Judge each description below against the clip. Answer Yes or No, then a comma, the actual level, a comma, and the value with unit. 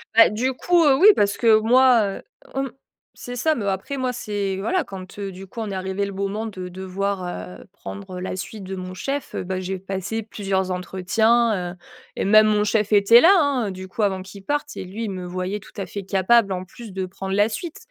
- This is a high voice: Yes, high, 200 Hz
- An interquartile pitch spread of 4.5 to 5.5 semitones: No, average, 3.2 semitones